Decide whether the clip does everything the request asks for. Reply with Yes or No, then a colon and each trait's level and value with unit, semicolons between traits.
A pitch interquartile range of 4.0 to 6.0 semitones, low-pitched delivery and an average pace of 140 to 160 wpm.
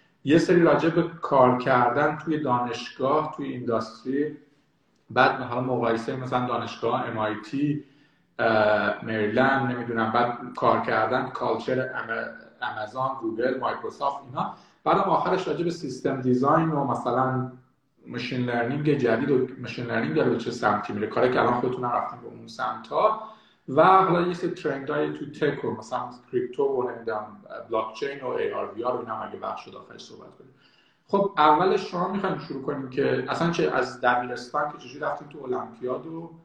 Yes: average, 4.4 semitones; low, 130 Hz; fast, 155 wpm